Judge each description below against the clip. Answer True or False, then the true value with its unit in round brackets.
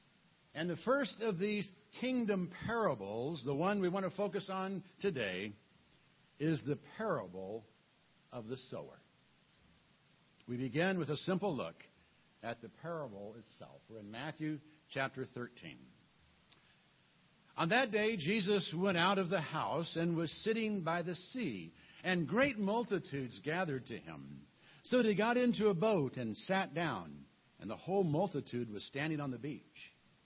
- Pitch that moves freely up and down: True (6.8 semitones)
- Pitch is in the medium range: True (165 Hz)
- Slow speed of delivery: False (150 wpm)